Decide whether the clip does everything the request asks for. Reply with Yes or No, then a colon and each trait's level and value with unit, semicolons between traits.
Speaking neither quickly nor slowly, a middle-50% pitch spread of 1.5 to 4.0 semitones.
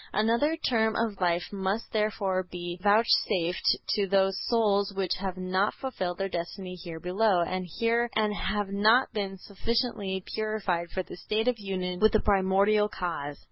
Yes: average, 150 wpm; average, 2.8 semitones